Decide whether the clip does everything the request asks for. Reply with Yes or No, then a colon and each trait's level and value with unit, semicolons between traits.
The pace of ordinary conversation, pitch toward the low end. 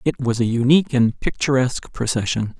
Yes: average, 160 wpm; low, 125 Hz